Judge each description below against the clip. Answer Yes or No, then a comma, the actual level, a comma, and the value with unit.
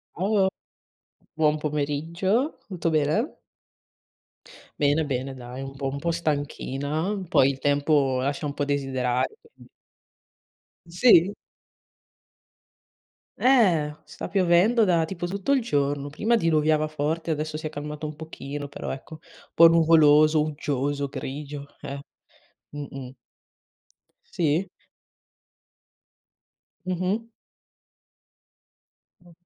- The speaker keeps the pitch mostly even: No, average, 3.3 semitones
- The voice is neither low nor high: Yes, medium, 155 Hz